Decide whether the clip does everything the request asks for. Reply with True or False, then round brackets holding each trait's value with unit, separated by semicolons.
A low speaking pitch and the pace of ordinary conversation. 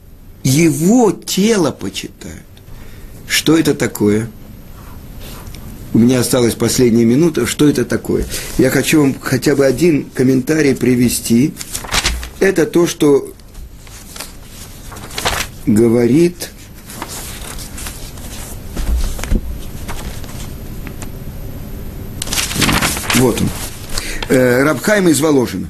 False (120 Hz; 70 wpm)